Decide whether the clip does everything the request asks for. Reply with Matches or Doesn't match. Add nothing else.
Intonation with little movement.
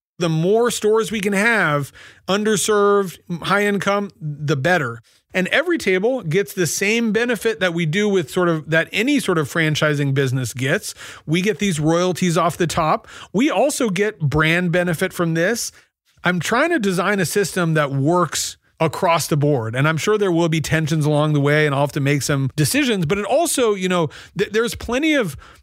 Doesn't match